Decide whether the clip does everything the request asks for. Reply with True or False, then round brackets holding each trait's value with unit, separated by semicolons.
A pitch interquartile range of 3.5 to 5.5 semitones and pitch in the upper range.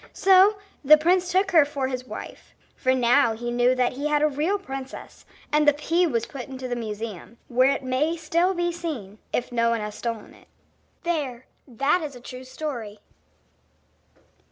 True (4.8 semitones; 270 Hz)